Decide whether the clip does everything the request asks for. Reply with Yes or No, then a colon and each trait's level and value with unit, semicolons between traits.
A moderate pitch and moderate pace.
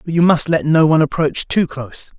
No: medium, 155 Hz; fast, 245 wpm